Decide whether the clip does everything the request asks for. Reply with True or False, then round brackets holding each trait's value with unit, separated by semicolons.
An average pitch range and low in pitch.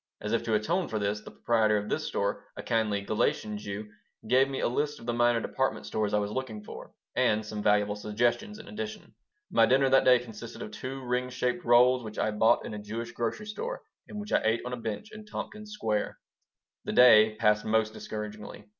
True (3.3 semitones; 115 Hz)